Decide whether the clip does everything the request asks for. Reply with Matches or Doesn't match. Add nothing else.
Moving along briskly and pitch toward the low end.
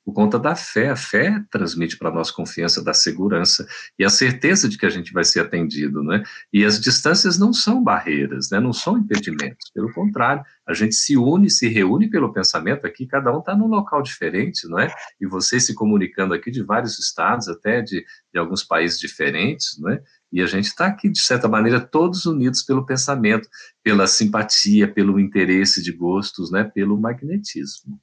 Matches